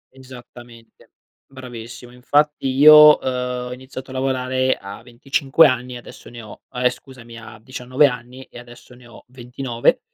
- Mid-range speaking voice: No, low, 125 Hz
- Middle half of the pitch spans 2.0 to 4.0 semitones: No, narrow, 1.5 semitones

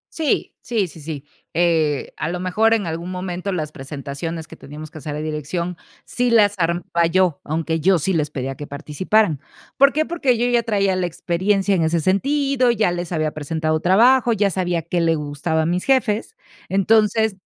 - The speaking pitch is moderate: Yes, medium, 175 Hz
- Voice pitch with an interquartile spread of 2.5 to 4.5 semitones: No, average, 5.0 semitones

